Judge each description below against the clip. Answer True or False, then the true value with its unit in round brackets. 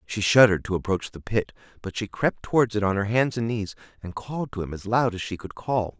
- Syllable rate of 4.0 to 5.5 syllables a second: False (5.8 syllables/s)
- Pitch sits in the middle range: False (105 Hz)